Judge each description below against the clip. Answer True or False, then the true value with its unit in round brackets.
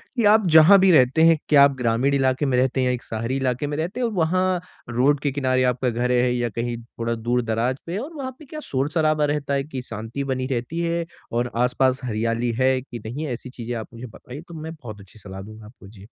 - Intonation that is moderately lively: True (4.6 semitones)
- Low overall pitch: True (130 Hz)